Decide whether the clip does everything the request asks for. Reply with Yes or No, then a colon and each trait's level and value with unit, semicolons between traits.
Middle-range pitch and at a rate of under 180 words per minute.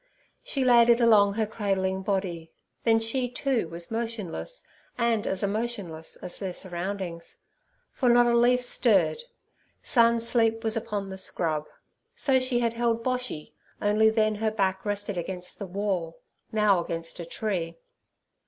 No: high, 210 Hz; average, 150 wpm